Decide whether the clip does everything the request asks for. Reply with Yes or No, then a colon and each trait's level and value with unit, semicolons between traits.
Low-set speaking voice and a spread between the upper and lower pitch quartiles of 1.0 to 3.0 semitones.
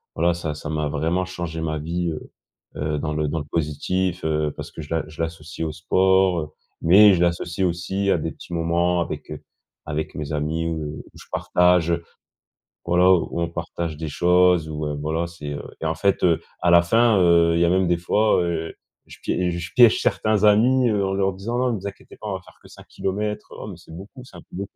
Yes: very low, 85 Hz; average, 2.7 semitones